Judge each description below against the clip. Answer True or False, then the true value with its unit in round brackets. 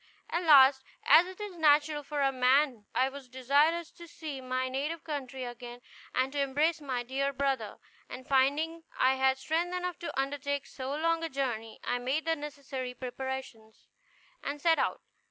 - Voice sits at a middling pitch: False (275 Hz)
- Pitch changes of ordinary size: True (3.1 semitones)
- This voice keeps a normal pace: True (170 wpm)